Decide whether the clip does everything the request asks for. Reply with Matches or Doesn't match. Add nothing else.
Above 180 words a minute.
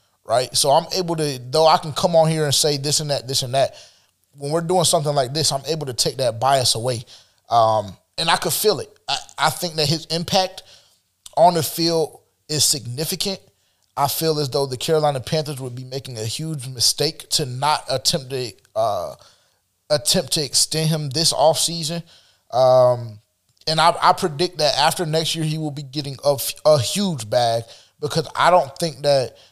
Matches